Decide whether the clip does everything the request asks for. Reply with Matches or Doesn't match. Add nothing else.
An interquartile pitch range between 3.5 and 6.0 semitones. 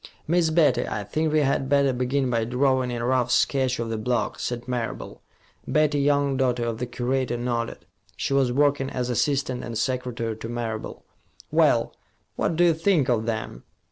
Doesn't match